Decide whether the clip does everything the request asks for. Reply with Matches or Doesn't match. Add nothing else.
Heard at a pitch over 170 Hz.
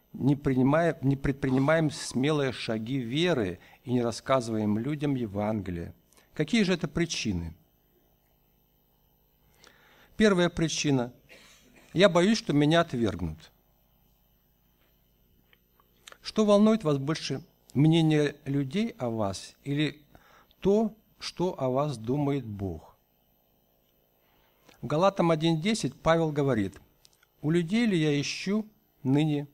Doesn't match